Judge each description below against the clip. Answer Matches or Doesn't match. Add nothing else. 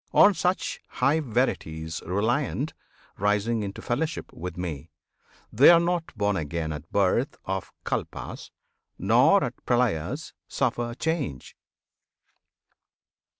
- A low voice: Matches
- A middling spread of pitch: Doesn't match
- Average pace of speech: Doesn't match